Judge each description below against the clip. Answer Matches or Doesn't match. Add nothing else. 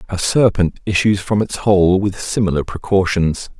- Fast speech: Doesn't match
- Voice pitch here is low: Matches